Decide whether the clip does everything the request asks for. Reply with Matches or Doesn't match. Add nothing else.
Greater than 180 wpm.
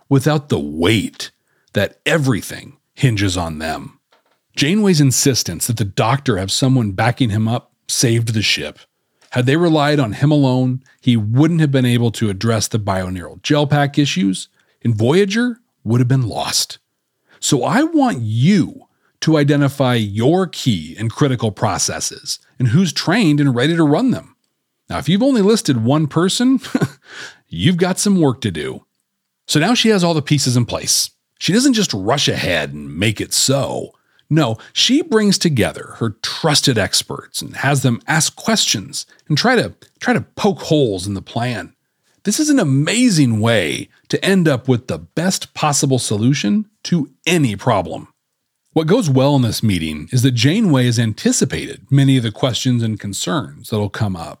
Doesn't match